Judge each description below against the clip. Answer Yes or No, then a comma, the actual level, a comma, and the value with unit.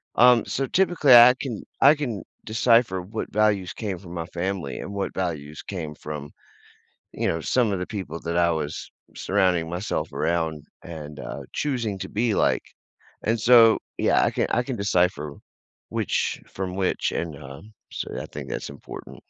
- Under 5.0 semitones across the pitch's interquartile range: No, wide, 5.6 semitones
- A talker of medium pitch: No, very low, 95 Hz